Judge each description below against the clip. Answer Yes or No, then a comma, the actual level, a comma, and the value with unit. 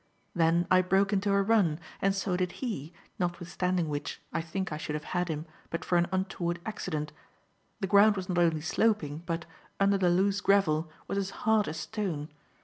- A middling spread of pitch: Yes, average, 3.2 semitones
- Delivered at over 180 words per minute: Yes, average, 190 wpm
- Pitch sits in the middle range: Yes, medium, 180 Hz